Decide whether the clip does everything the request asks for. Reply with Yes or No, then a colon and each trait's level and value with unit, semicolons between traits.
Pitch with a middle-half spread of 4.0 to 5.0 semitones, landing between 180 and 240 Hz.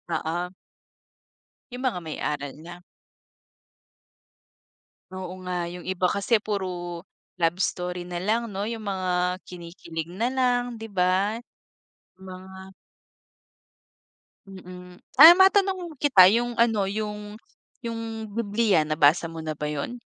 Yes: average, 4.5 semitones; high, 190 Hz